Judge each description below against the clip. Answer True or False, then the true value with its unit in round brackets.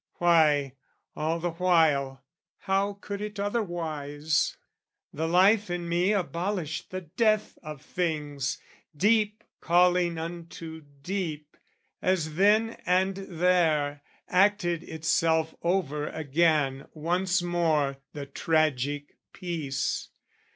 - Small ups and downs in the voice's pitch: False (3.5 semitones)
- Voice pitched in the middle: True (170 Hz)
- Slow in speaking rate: True (100 wpm)